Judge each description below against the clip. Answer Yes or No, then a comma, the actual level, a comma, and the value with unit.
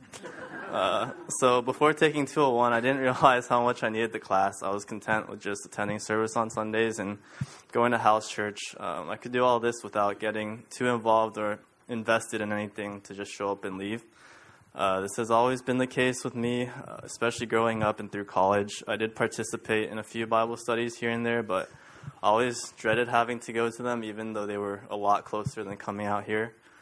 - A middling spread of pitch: No, narrow, 2.3 semitones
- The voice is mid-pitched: No, low, 115 Hz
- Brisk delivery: Yes, fast, 210 wpm